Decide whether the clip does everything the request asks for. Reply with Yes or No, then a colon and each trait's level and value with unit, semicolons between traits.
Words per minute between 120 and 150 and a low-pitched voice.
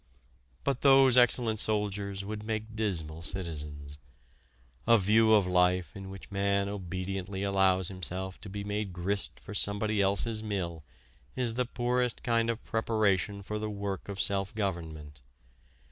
Yes: average, 145 wpm; low, 100 Hz